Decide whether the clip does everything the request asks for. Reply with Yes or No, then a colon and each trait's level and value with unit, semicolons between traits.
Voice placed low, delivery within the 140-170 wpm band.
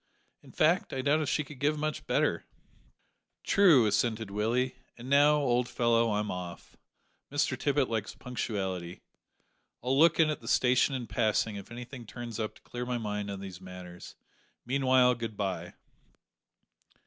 Yes: low, 120 Hz; average, 155 wpm